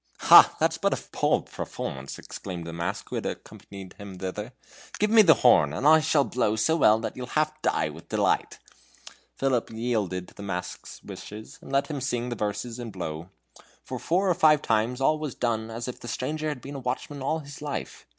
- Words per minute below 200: No, fast, 205 wpm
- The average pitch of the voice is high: No, low, 120 Hz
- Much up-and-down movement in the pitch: Yes, wide, 6.2 semitones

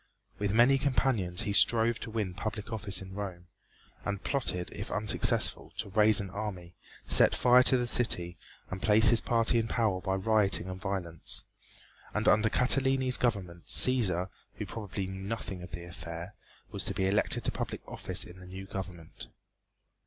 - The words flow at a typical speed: Yes, average, 170 wpm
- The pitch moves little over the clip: No, average, 3.6 semitones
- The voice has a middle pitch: No, low, 100 Hz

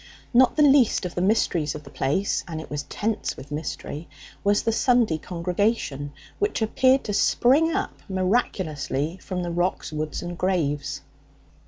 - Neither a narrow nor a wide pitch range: No, wide, 6.7 semitones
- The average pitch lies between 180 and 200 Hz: Yes, medium, 185 Hz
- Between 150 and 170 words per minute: Yes, average, 160 wpm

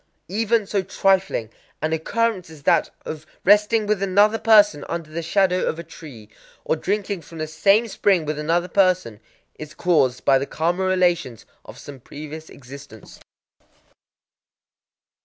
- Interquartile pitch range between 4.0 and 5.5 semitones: Yes, average, 4.4 semitones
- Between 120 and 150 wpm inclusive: Yes, average, 145 wpm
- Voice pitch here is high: No, medium, 170 Hz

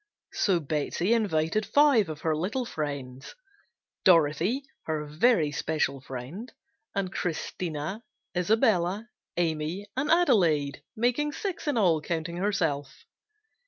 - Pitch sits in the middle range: Yes, medium, 175 Hz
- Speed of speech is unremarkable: No, slow, 110 wpm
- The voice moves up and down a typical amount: No, wide, 6.4 semitones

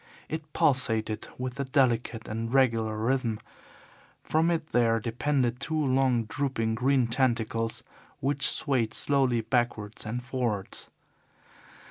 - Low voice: Yes, low, 125 Hz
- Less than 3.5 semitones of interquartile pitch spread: Yes, average, 3.0 semitones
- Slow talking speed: Yes, slow, 115 wpm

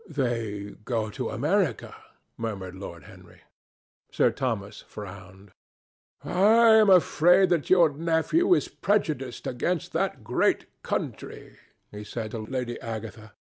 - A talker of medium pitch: No, low, 125 Hz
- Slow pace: Yes, slow, 120 wpm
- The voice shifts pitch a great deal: Yes, wide, 8.6 semitones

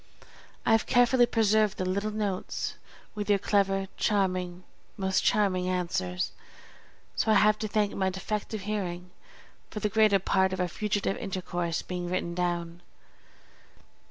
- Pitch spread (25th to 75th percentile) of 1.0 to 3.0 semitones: Yes, average, 2.7 semitones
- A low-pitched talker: No, high, 195 Hz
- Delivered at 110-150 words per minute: Yes, average, 140 wpm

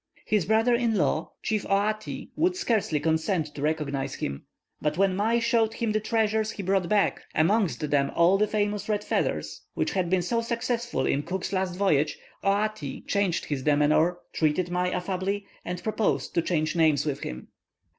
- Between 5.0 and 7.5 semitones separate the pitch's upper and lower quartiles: Yes, wide, 5.4 semitones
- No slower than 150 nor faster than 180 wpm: Yes, average, 175 wpm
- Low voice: No, high, 190 Hz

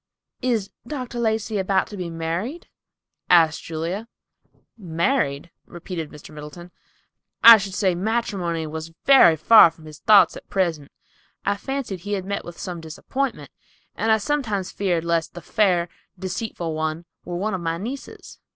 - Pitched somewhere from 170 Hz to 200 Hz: Yes, medium, 185 Hz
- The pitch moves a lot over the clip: No, average, 4.8 semitones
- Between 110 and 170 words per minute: Yes, average, 150 wpm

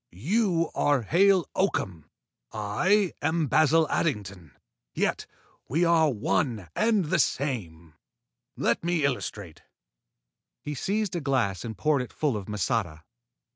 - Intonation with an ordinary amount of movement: No, wide, 8.5 semitones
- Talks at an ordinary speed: No, slow, 125 wpm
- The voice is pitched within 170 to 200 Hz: No, medium, 140 Hz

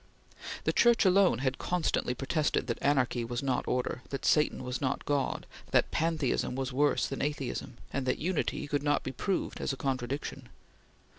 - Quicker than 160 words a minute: Yes, average, 170 wpm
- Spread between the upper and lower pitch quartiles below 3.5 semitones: Yes, average, 2.8 semitones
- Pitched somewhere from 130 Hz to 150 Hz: Yes, low, 135 Hz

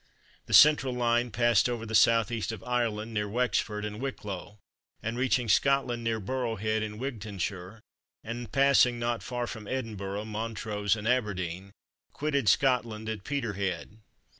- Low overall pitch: Yes, low, 115 Hz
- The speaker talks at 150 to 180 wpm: No, average, 140 wpm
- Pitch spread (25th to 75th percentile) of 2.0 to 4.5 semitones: Yes, average, 2.8 semitones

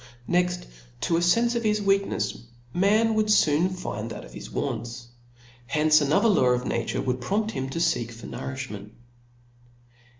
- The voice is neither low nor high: Yes, medium, 165 Hz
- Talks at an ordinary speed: Yes, average, 165 wpm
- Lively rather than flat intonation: Yes, wide, 8.2 semitones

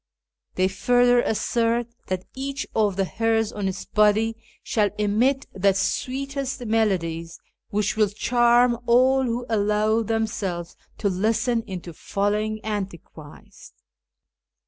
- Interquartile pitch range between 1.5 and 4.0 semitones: Yes, average, 3.3 semitones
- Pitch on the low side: No, high, 215 Hz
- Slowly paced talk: Yes, slow, 115 wpm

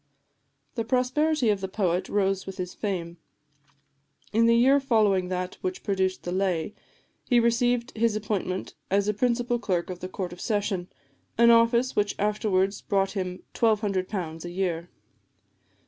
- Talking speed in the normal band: Yes, average, 150 wpm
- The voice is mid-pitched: No, high, 200 Hz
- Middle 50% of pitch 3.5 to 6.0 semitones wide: Yes, average, 3.9 semitones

